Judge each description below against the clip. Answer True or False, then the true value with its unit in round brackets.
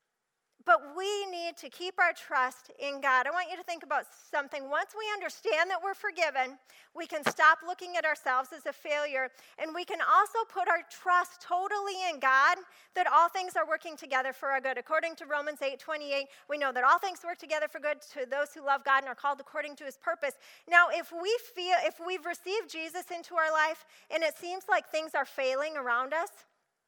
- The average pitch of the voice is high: True (320 Hz)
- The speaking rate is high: True (215 wpm)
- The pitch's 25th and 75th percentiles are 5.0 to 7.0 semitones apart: False (3.9 semitones)